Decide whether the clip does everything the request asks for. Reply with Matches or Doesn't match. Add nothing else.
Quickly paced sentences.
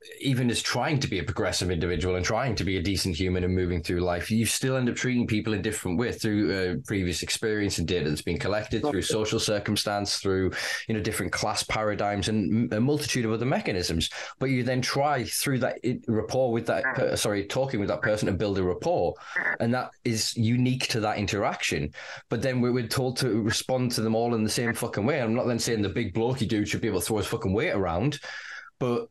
Matches